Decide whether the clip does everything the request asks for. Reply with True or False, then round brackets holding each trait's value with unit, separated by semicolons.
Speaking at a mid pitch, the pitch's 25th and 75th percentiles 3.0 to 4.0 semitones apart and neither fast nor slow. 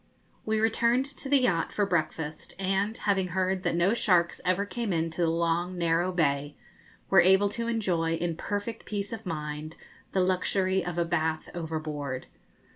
True (180 Hz; 3.6 semitones; 165 wpm)